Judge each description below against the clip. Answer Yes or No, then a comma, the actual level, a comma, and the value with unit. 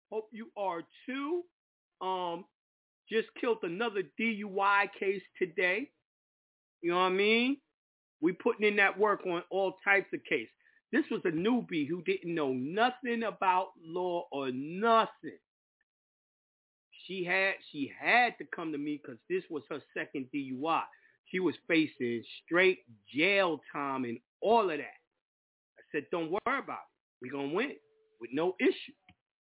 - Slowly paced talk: No, average, 155 wpm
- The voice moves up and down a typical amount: No, wide, 7.0 semitones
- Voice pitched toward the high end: Yes, high, 200 Hz